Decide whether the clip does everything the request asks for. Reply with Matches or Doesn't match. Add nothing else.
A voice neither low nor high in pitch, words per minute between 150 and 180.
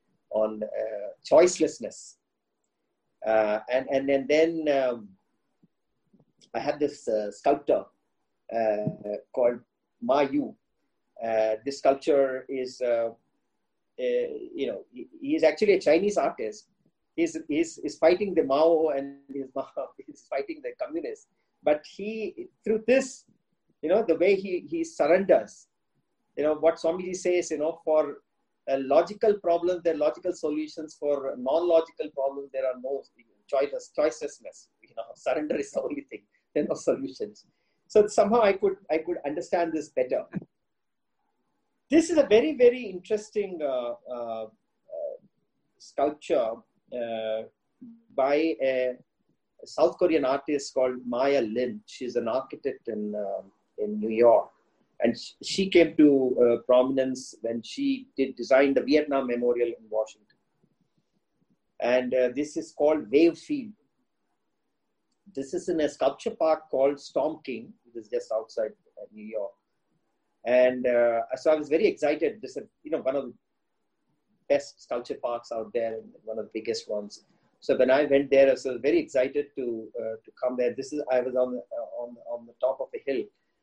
Matches